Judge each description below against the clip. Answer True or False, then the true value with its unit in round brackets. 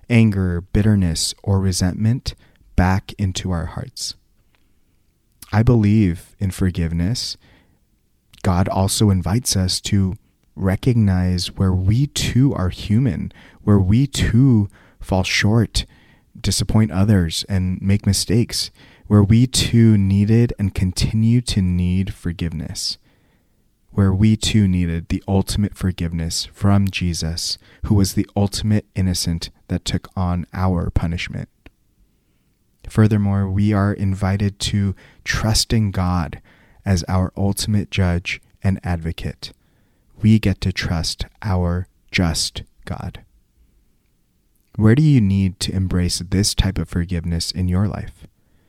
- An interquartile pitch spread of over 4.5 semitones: False (2.9 semitones)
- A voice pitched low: True (95 Hz)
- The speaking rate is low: True (115 wpm)